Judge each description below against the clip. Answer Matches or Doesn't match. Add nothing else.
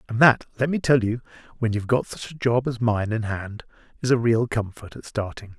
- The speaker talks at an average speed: Doesn't match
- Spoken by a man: Matches